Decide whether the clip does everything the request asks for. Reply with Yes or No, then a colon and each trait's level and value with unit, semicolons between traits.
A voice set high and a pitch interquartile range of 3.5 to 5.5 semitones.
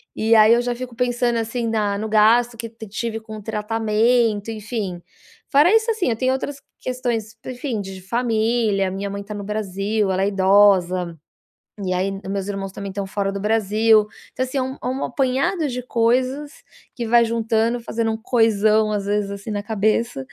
No: high, 220 Hz; average, 3.0 semitones